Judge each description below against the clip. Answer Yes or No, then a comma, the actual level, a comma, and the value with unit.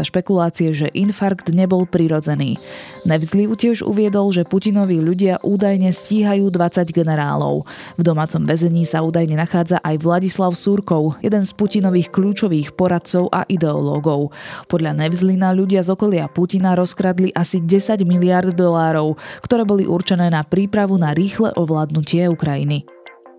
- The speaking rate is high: No, average, 130 wpm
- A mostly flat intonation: No, average, 3.2 semitones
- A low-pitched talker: No, medium, 180 Hz